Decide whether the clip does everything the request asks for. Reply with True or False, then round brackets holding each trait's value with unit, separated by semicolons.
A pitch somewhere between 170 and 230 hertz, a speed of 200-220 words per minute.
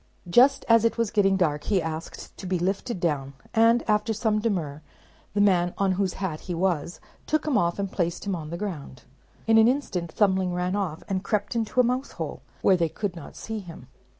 True (190 Hz; 205 wpm)